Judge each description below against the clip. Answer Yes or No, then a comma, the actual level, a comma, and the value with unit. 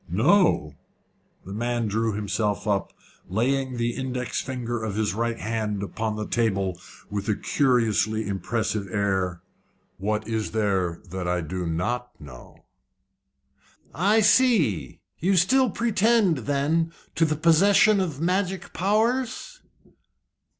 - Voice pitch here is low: Yes, low, 115 Hz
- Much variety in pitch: Yes, wide, 8.5 semitones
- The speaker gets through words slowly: Yes, slow, 120 wpm